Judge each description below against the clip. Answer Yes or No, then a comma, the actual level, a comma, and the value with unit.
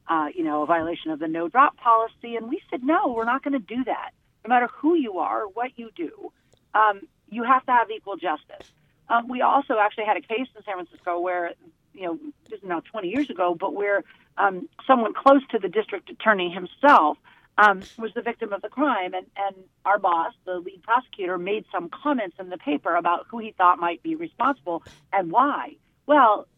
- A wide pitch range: Yes, wide, 6.0 semitones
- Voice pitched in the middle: No, high, 215 Hz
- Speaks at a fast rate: Yes, fast, 210 wpm